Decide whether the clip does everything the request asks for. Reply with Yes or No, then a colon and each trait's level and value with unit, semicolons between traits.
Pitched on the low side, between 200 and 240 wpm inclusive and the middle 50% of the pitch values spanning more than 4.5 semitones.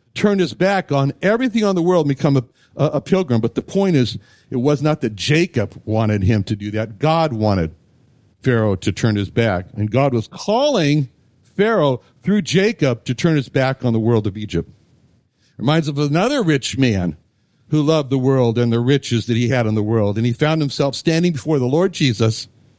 Yes: low, 130 Hz; fast, 205 wpm; average, 5.1 semitones